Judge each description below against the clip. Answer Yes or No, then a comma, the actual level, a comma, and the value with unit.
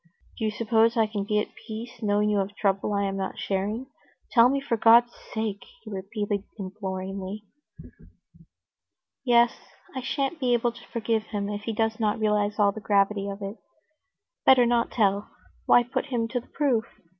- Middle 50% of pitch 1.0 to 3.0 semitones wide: Yes, average, 2.7 semitones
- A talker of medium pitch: No, high, 215 Hz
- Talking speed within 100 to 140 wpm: No, average, 180 wpm